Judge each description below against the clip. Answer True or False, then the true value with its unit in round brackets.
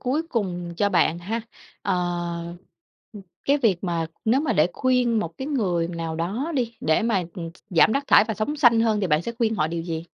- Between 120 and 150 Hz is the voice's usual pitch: False (205 Hz)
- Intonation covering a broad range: True (5.7 semitones)